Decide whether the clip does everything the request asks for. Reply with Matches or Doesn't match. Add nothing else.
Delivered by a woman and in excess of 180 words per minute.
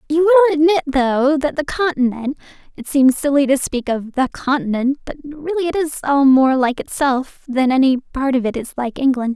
Matches